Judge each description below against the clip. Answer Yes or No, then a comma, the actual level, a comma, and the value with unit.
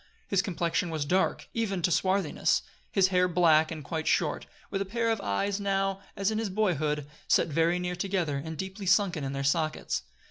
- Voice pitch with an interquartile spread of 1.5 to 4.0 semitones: Yes, average, 3.6 semitones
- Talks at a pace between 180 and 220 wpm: Yes, average, 190 wpm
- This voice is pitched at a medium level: Yes, medium, 180 Hz